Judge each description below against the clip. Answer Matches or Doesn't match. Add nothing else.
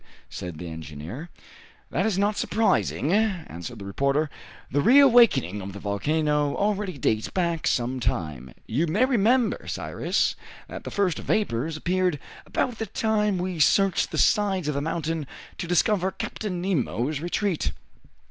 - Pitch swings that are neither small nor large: Doesn't match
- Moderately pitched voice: Matches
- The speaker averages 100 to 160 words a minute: Matches